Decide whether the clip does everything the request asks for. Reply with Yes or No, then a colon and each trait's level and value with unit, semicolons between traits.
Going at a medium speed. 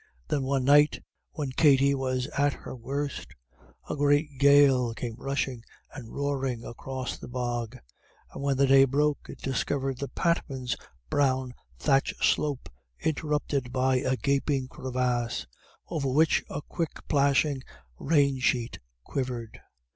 No: slow, 130 wpm